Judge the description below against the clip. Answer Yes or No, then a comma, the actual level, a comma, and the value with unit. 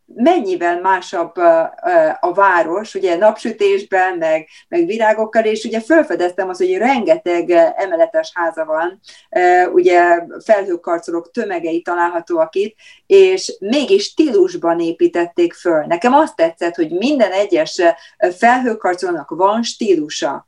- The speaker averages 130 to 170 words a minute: No, average, 110 wpm